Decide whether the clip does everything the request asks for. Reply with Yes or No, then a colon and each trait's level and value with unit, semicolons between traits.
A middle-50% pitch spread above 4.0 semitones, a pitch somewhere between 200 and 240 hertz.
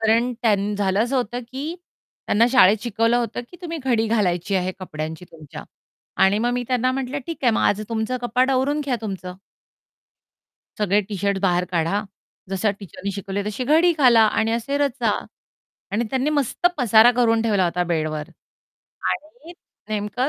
Yes: average, 4.4 semitones; high, 225 Hz